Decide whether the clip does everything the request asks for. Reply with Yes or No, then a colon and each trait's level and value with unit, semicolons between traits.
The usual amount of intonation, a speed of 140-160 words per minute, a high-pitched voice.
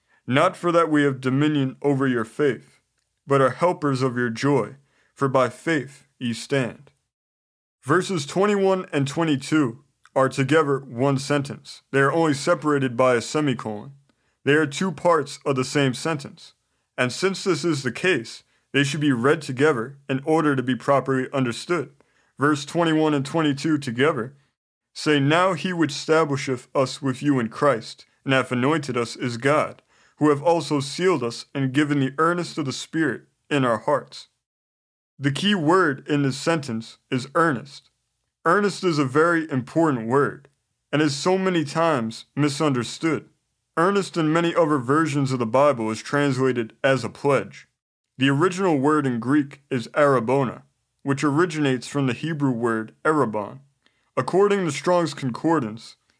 No: average, 3.4 semitones; average, 155 wpm; medium, 140 Hz